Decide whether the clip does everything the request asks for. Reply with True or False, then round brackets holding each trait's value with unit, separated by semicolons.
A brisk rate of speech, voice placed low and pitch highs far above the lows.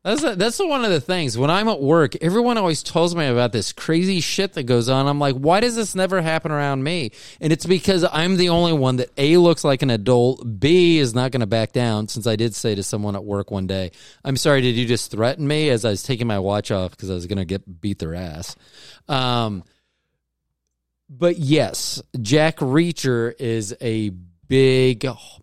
True (215 wpm; 130 Hz; 6.4 semitones)